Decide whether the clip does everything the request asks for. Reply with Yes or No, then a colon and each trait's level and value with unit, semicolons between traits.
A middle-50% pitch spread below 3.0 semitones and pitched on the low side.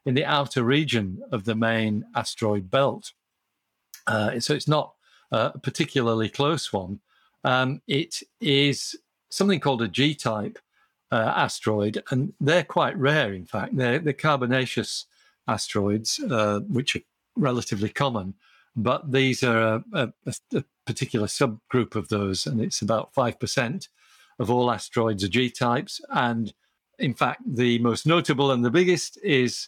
No: average, 4.2 semitones; low, 125 Hz